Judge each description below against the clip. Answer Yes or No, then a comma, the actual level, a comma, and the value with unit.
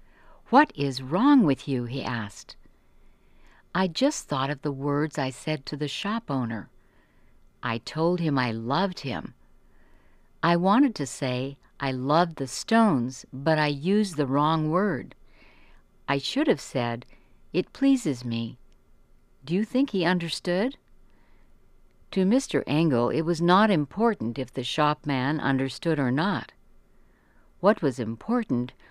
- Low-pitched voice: No, medium, 145 Hz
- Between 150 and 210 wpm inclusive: No, average, 140 wpm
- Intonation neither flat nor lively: No, wide, 5.9 semitones